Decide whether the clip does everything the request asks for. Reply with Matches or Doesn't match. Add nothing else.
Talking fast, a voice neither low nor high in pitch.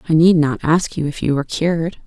Matches